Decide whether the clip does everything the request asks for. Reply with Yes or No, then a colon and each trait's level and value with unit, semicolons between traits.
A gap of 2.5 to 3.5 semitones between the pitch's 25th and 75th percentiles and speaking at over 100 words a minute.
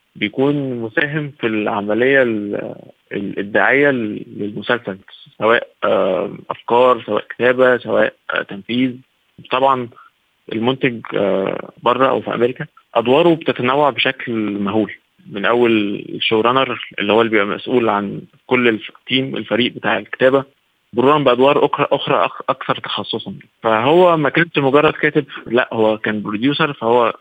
No: average, 4.0 semitones; average, 115 wpm